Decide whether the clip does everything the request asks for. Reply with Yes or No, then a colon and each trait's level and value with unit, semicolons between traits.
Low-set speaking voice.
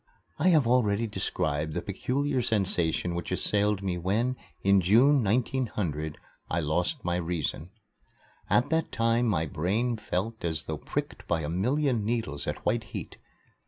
Yes: low, 105 Hz